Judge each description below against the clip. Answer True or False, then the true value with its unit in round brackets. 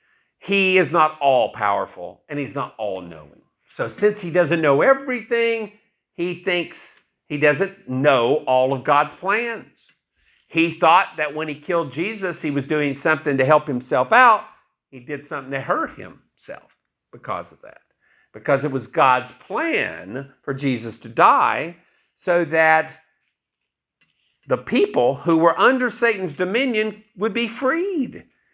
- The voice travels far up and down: True (6.4 semitones)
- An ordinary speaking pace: True (145 wpm)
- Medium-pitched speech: True (165 Hz)